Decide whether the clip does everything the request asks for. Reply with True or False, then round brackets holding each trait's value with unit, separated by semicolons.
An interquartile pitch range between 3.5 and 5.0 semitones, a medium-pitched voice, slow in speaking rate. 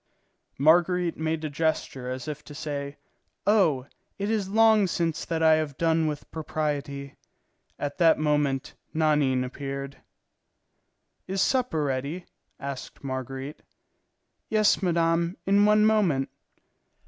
True (4.1 semitones; 155 Hz; 120 wpm)